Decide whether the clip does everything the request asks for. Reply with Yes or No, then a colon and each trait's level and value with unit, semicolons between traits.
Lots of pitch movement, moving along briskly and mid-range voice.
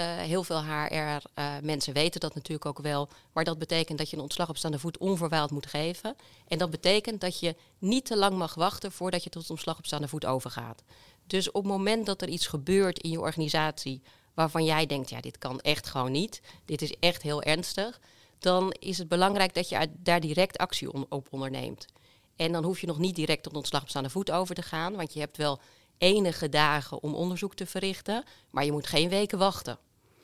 No: average, 3.6 semitones; fast, 215 wpm; medium, 160 Hz